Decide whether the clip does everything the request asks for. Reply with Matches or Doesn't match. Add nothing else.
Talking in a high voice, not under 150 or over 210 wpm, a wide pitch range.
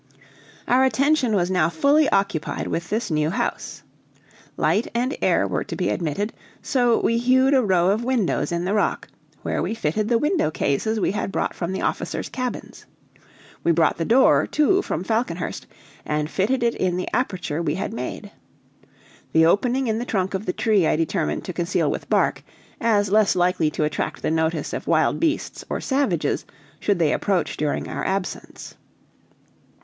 Matches